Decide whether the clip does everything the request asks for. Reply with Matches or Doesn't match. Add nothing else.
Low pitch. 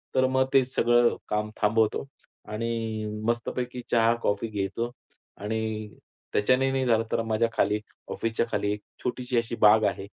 Matches